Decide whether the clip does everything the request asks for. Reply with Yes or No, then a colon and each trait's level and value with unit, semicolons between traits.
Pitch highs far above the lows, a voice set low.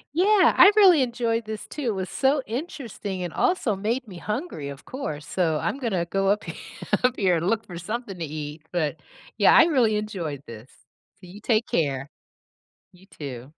No: wide, 6.9 semitones; high, 205 Hz